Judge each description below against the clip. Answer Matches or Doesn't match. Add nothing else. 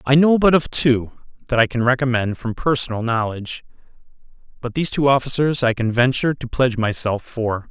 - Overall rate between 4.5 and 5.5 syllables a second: Doesn't match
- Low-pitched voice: Matches